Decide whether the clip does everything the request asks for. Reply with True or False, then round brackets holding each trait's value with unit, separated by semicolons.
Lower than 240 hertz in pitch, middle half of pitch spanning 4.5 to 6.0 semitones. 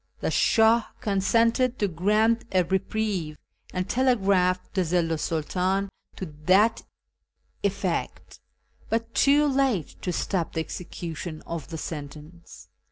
True (190 Hz; 4.8 semitones)